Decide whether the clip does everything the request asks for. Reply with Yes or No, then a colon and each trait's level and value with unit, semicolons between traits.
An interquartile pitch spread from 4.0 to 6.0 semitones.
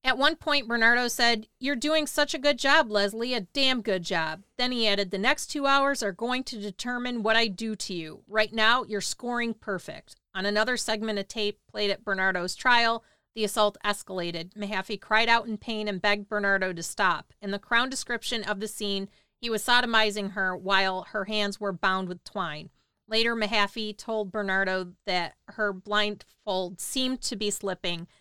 No: average, 3.2 semitones